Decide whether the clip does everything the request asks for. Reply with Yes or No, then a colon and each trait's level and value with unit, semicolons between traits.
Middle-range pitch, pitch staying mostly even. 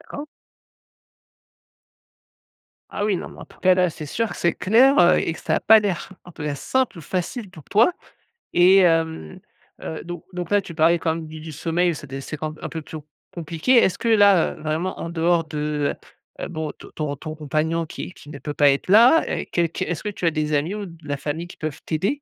No: medium, 165 Hz; average, 3.3 semitones